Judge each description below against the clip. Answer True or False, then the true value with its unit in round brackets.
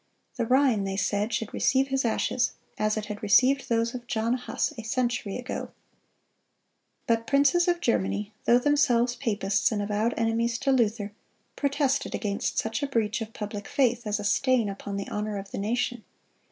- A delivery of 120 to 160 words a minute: False (175 wpm)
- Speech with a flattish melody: False (3.4 semitones)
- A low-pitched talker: False (230 Hz)